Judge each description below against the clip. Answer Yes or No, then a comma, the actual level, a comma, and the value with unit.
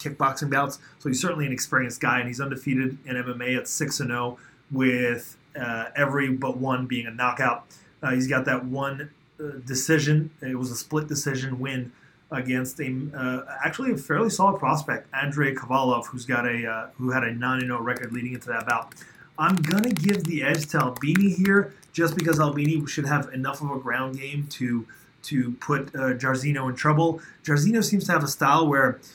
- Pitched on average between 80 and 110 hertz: No, low, 135 Hz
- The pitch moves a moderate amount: Yes, average, 3.1 semitones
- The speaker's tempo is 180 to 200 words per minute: Yes, average, 190 wpm